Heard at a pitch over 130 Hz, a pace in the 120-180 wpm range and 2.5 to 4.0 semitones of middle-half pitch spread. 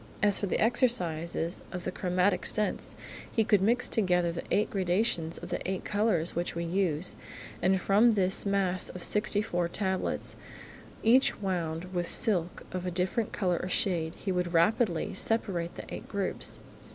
Yes: medium, 185 Hz; average, 165 wpm; average, 2.9 semitones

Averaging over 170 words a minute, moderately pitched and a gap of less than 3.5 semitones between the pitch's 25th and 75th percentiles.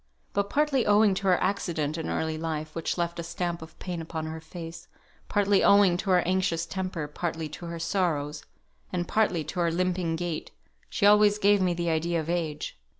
Yes: average, 195 wpm; medium, 175 Hz; average, 2.7 semitones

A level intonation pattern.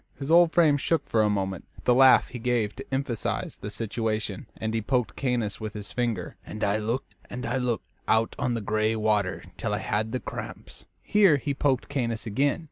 No: average, 3.6 semitones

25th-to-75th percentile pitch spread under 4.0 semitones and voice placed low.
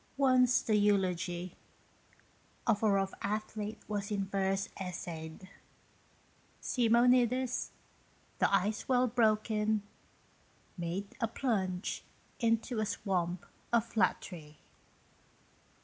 No: average, 3.4 semitones; high, 210 Hz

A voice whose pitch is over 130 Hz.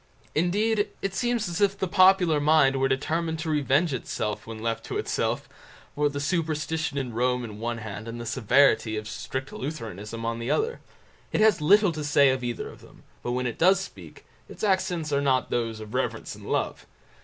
Yes: medium, 140 Hz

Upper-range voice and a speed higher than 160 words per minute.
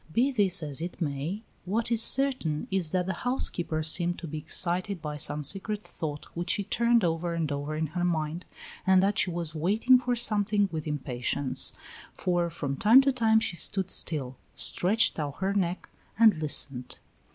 No: medium, 175 Hz; average, 180 wpm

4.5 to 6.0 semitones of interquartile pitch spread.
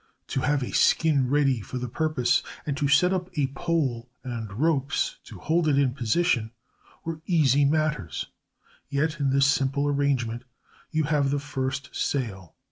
No: average, 3.3 semitones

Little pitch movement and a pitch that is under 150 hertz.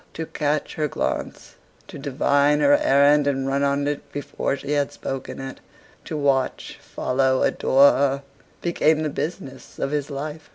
Yes: narrow, 1.5 semitones; medium, 140 Hz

